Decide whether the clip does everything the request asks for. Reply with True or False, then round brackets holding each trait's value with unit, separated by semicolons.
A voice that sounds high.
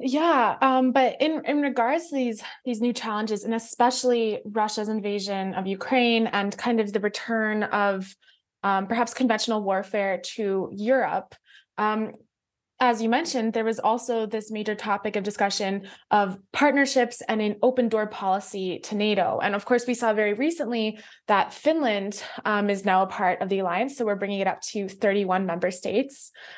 True (215 Hz)